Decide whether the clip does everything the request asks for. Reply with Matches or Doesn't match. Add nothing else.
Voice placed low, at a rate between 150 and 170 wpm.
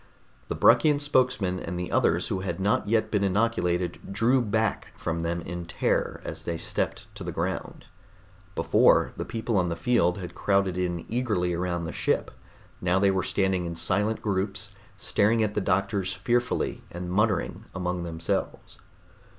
Matches